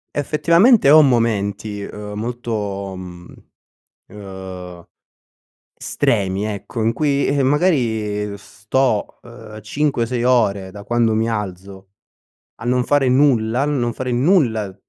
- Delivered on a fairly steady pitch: No, average, 4.3 semitones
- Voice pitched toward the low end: Yes, low, 110 Hz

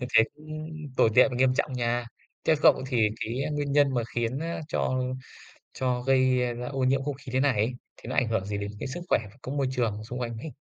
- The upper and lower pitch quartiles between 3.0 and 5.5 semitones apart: No, narrow, 2.6 semitones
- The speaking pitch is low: Yes, low, 130 Hz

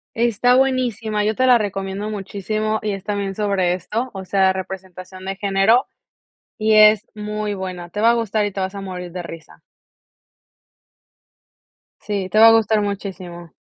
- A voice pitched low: No, high, 205 Hz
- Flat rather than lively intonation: Yes, narrow, 2.3 semitones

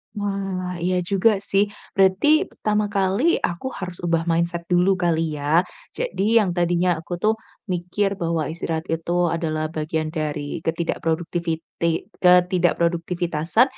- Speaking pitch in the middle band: Yes, medium, 175 Hz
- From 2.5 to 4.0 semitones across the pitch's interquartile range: Yes, average, 2.8 semitones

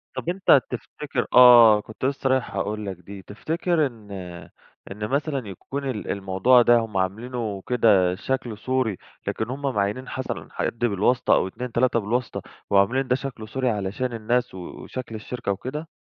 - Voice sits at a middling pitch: No, low, 120 Hz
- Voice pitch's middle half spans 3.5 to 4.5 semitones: Yes, average, 3.9 semitones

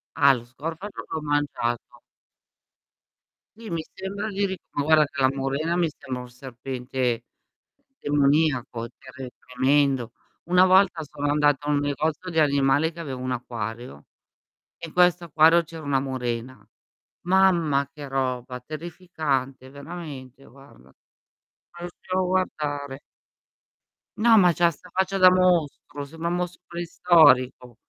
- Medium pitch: Yes, medium, 145 Hz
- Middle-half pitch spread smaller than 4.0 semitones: No, average, 4.6 semitones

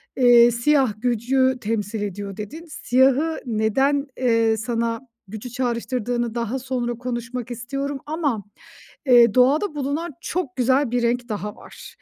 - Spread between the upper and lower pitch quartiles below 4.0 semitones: Yes, average, 2.8 semitones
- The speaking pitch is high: Yes, high, 245 Hz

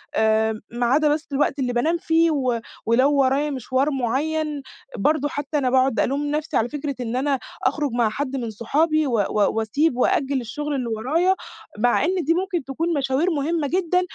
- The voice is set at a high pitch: Yes, very high, 275 Hz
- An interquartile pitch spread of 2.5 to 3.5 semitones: No, average, 3.9 semitones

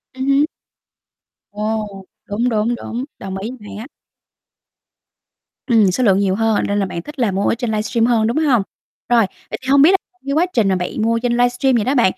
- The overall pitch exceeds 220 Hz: Yes, high, 230 Hz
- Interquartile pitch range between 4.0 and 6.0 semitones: No, average, 3.4 semitones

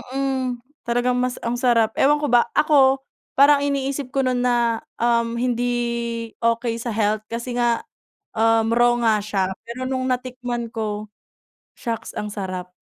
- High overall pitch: Yes, high, 240 Hz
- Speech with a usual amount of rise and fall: No, narrow, 1.8 semitones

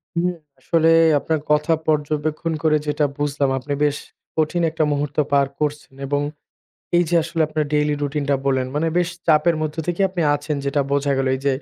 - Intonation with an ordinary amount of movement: No, narrow, 2.0 semitones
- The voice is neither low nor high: Yes, medium, 150 Hz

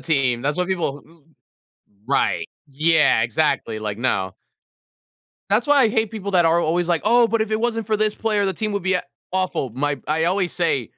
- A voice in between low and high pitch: Yes, medium, 175 Hz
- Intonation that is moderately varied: No, wide, 6.9 semitones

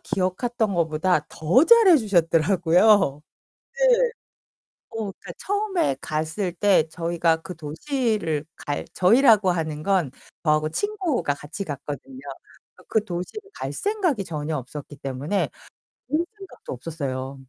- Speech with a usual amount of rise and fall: No, wide, 6.8 semitones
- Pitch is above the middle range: No, medium, 180 Hz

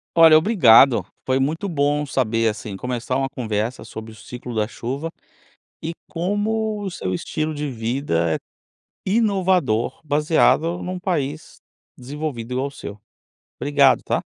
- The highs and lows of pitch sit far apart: Yes, wide, 5.9 semitones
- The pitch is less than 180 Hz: Yes, medium, 140 Hz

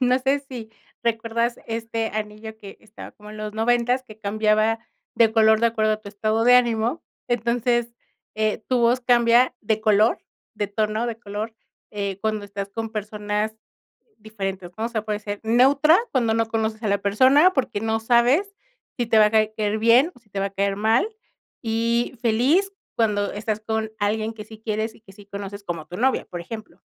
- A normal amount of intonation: No, narrow, 2.0 semitones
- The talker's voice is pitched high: Yes, high, 220 Hz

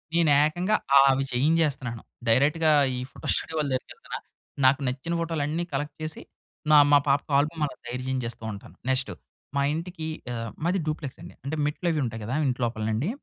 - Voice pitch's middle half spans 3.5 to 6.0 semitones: Yes, average, 3.9 semitones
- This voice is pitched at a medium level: Yes, medium, 145 Hz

